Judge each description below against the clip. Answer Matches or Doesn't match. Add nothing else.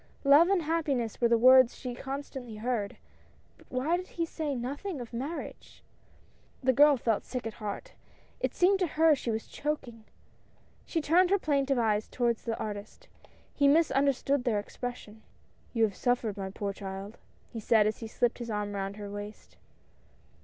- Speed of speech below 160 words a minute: Doesn't match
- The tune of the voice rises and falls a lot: Doesn't match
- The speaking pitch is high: Matches